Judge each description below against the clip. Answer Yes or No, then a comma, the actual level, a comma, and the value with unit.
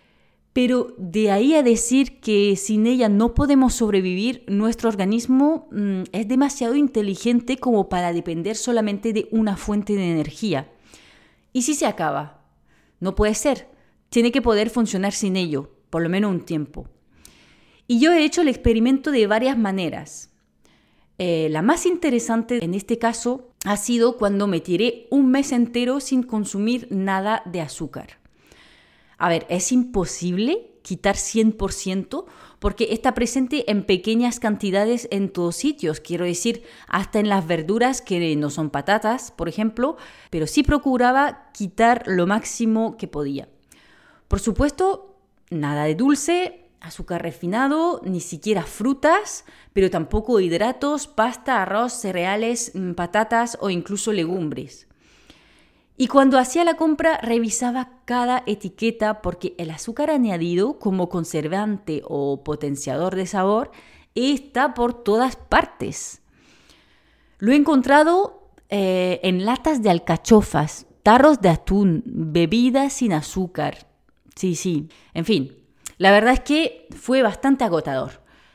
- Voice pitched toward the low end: No, high, 220 Hz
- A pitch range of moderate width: No, wide, 5.7 semitones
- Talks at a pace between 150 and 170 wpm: No, average, 135 wpm